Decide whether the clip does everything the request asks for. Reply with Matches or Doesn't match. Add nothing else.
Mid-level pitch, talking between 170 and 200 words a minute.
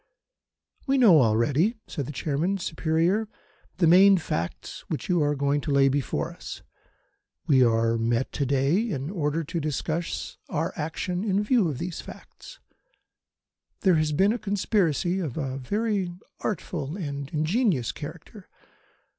Doesn't match